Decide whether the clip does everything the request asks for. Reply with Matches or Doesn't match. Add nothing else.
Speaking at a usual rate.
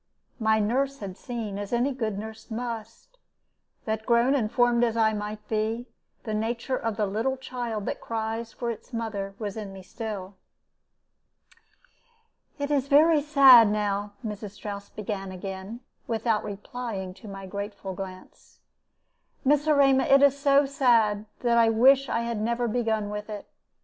Matches